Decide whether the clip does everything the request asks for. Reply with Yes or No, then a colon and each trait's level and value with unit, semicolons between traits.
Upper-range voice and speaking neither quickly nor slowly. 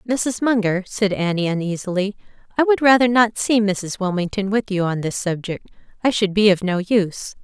Yes: high, 205 Hz; average, 185 wpm